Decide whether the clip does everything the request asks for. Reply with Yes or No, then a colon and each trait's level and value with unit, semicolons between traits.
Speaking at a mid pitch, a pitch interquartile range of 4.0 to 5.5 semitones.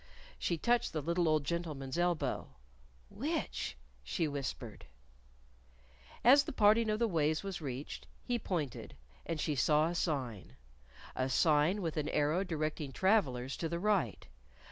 Yes: medium, 160 Hz; average, 4.6 semitones